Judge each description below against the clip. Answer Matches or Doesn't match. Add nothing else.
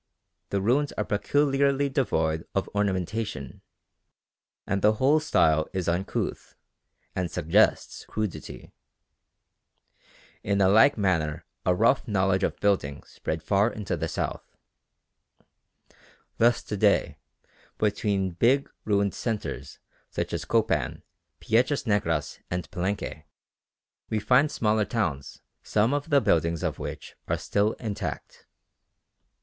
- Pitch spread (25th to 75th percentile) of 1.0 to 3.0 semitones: Doesn't match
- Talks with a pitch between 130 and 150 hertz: Doesn't match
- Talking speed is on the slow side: Matches